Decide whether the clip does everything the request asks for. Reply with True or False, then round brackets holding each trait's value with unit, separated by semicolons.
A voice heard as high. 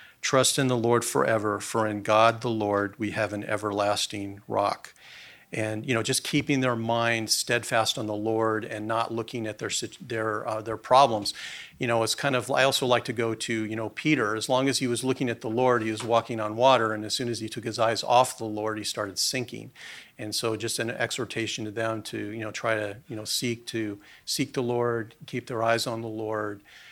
False (115 Hz)